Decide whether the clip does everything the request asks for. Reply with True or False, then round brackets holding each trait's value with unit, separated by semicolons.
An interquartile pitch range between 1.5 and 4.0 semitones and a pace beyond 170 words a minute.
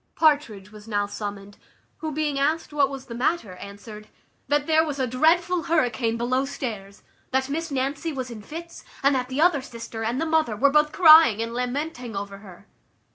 False (5.5 semitones; 185 wpm)